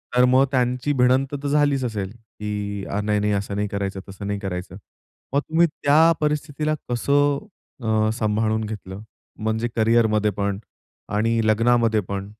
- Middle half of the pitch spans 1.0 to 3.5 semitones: No, average, 4.2 semitones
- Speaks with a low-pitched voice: Yes, low, 110 Hz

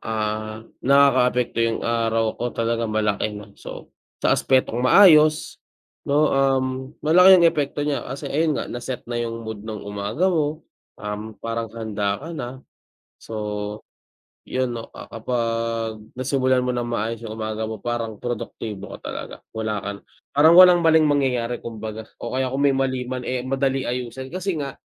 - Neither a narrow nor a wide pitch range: Yes, average, 3.7 semitones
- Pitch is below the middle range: Yes, low, 120 Hz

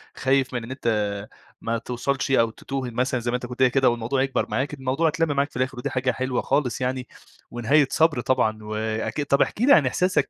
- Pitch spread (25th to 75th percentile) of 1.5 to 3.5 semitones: Yes, narrow, 2.4 semitones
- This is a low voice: Yes, low, 130 Hz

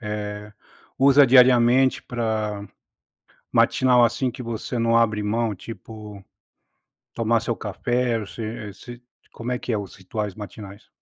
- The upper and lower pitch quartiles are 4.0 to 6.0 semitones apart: No, narrow, 2.5 semitones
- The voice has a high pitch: No, low, 115 Hz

